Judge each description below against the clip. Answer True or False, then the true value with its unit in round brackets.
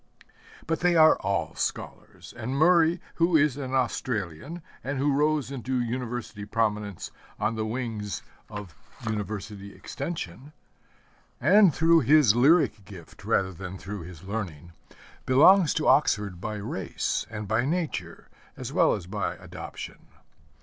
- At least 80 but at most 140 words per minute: True (135 wpm)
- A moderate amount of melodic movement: False (6.7 semitones)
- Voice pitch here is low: True (115 Hz)